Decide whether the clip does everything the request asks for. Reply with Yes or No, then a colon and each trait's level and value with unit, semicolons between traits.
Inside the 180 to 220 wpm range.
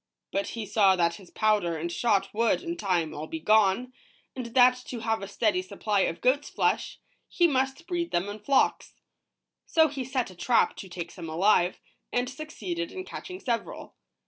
Yes: average, 185 wpm